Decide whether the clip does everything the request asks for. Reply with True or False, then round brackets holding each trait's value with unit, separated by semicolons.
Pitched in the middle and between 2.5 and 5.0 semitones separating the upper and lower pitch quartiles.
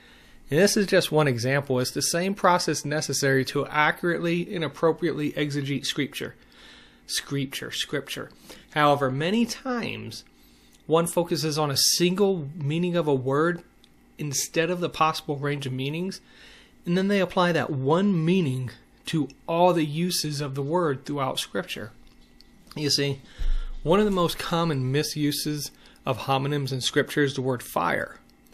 True (150 Hz; 4.0 semitones)